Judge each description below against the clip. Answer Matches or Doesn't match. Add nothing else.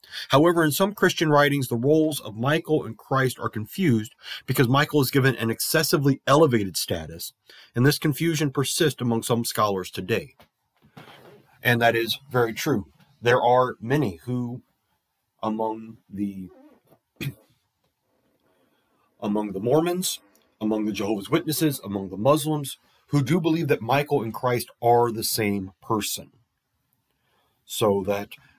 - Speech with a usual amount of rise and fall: Matches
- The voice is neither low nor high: Doesn't match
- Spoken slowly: Matches